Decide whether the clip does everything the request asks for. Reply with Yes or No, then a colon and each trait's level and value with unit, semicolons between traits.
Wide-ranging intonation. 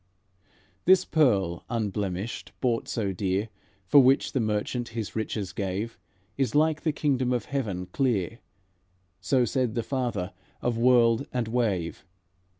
No: average, 4.1 semitones